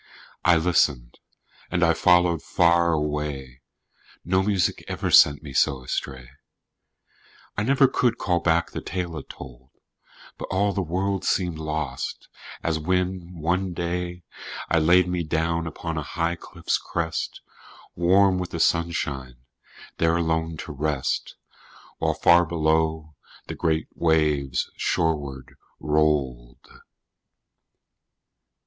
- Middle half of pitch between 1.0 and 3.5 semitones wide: Yes, average, 2.8 semitones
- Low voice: Yes, very low, 80 Hz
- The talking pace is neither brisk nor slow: No, slow, 120 wpm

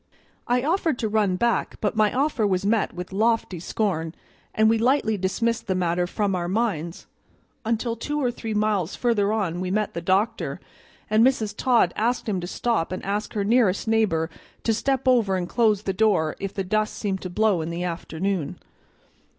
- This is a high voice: Yes, high, 210 Hz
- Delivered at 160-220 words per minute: Yes, average, 190 wpm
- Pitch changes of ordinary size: Yes, average, 3.8 semitones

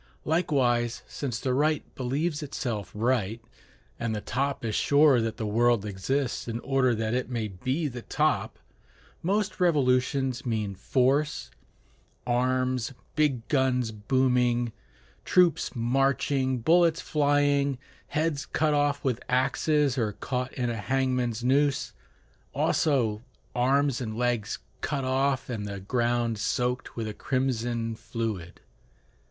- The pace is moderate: No, slow, 125 wpm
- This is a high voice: No, low, 125 Hz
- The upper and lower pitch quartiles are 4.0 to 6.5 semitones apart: No, average, 3.3 semitones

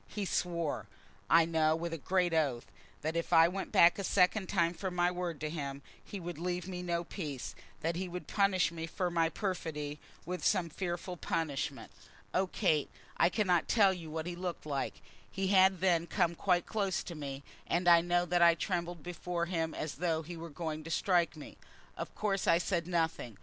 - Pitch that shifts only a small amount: Yes, narrow, 1.9 semitones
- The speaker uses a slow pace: No, average, 200 wpm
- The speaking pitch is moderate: Yes, medium, 170 Hz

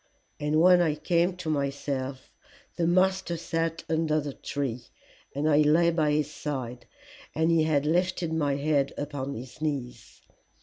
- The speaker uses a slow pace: No, average, 150 wpm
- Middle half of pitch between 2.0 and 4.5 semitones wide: Yes, average, 2.9 semitones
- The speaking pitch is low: No, medium, 150 Hz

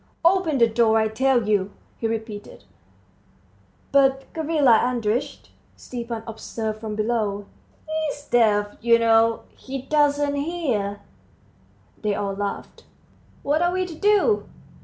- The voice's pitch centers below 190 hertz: No, high, 235 Hz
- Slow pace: Yes, slow, 120 wpm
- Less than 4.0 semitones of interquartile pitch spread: No, average, 5.0 semitones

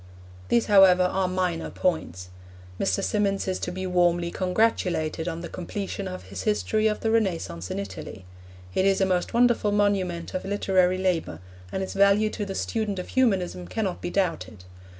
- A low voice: No, medium, 185 Hz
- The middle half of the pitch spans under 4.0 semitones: Yes, average, 2.7 semitones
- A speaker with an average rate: Yes, average, 170 wpm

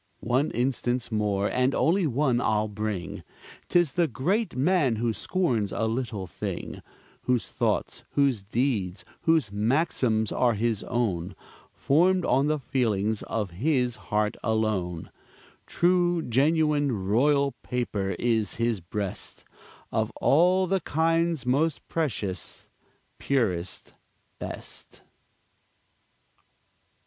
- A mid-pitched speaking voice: No, low, 120 Hz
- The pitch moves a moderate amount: No, wide, 6.0 semitones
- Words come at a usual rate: No, slow, 110 wpm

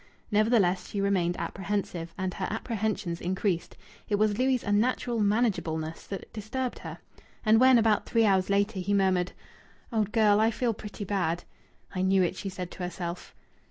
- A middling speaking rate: Yes, average, 160 wpm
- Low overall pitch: No, high, 200 Hz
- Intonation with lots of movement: No, average, 3.0 semitones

